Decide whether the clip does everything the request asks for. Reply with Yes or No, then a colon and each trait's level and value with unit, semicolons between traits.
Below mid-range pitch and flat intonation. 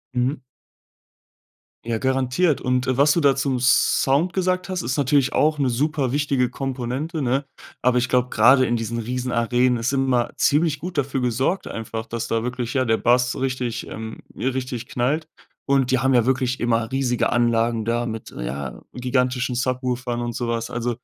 Yes: low, 125 Hz; narrow, 2.2 semitones